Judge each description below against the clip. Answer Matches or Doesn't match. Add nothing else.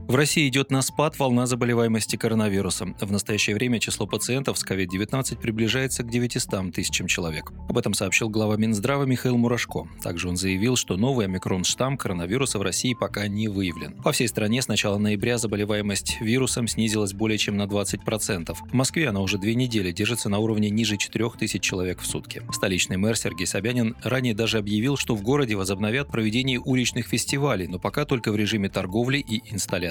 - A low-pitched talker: Matches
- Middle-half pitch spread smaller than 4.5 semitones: Matches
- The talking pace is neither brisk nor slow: Doesn't match